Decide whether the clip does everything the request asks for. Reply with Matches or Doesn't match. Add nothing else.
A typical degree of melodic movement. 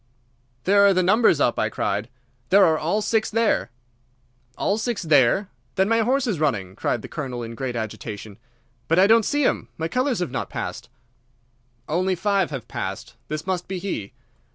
Doesn't match